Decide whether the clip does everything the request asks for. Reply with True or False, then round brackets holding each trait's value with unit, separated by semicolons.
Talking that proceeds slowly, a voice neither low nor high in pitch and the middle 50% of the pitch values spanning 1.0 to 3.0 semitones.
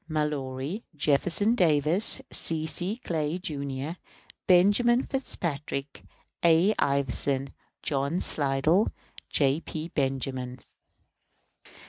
False (80 wpm; 155 Hz; 4.4 semitones)